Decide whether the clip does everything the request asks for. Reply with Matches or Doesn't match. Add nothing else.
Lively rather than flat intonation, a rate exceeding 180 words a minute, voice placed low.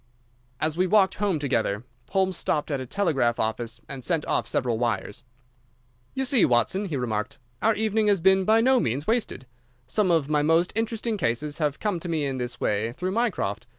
Doesn't match